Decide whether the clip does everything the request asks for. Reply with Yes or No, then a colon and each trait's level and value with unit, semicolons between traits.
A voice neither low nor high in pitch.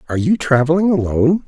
Yes: medium, 150 Hz